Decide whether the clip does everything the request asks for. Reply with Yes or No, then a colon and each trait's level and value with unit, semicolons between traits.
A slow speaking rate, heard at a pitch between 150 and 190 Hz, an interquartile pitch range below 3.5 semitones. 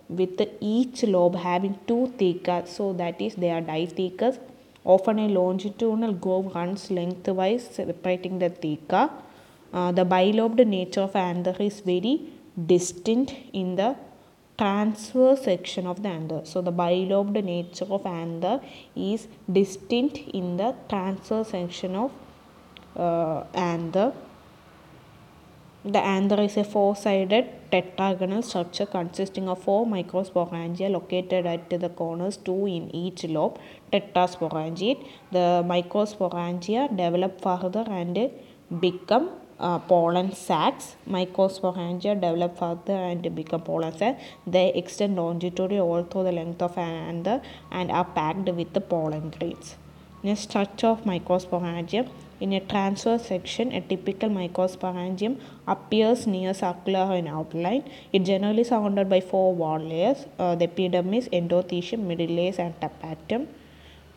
Yes: slow, 125 wpm; medium, 185 Hz; average, 2.8 semitones